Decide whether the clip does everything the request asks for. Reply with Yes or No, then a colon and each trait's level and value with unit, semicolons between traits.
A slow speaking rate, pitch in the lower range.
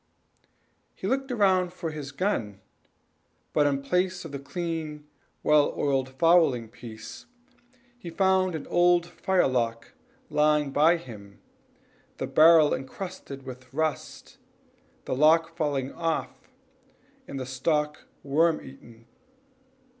No: slow, 115 wpm; medium, 150 Hz